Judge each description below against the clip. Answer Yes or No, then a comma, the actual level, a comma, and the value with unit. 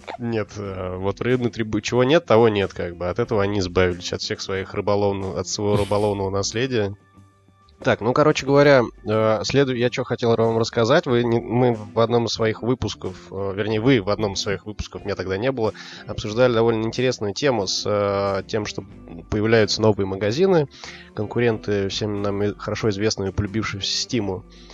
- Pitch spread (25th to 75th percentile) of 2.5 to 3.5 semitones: Yes, average, 3.0 semitones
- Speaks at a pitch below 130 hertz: Yes, low, 105 Hz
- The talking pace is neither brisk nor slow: No, fast, 165 wpm